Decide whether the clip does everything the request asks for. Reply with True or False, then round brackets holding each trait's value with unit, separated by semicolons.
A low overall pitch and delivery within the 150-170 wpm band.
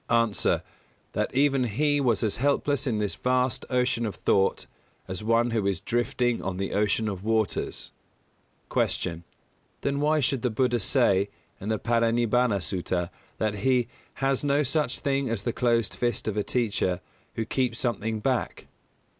True (115 Hz; 165 wpm)